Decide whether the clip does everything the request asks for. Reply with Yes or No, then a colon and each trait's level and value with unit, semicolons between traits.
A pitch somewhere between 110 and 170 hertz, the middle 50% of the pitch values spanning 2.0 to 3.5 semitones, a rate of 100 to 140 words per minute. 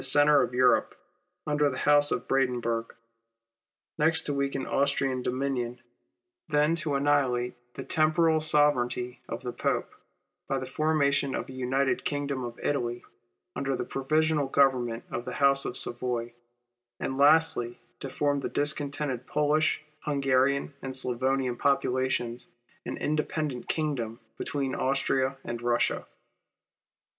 Yes: low, 135 Hz; average, 2.7 semitones; slow, 135 wpm